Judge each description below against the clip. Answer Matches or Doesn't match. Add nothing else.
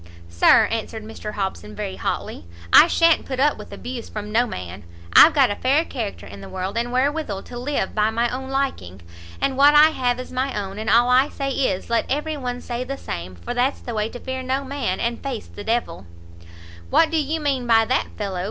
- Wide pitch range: Doesn't match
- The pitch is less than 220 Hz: Doesn't match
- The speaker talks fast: Matches